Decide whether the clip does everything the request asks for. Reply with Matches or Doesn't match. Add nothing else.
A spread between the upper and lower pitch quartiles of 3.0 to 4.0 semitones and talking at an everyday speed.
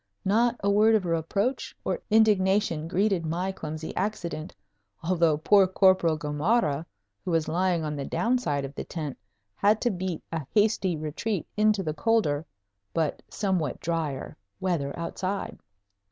Doesn't match